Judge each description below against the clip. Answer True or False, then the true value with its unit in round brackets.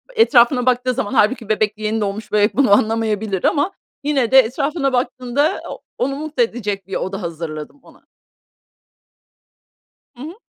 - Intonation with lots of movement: False (4.5 semitones)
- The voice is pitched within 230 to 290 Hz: True (235 Hz)